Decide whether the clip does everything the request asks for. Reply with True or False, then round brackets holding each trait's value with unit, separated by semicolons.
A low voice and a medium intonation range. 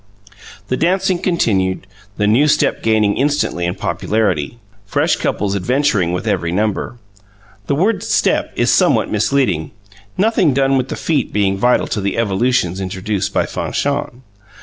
False (110 Hz; 6.3 semitones)